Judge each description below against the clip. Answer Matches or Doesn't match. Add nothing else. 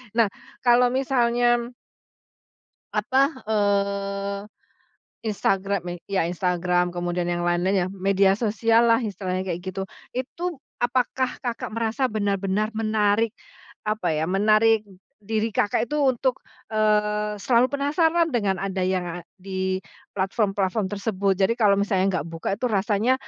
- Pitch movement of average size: Matches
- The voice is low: Doesn't match